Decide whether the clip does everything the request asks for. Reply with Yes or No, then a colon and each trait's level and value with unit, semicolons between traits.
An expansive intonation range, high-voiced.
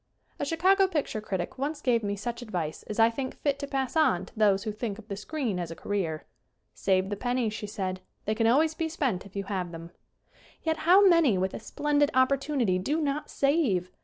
Yes: wide, 6.8 semitones; high, 230 Hz